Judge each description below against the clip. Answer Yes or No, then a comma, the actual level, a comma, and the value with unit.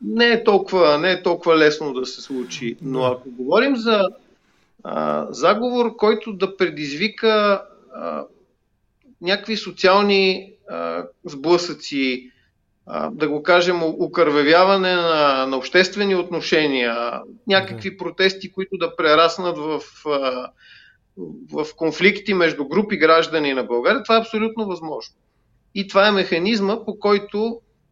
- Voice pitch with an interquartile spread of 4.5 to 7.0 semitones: Yes, wide, 5.4 semitones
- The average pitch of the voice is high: No, medium, 180 Hz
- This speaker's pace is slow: Yes, slow, 125 wpm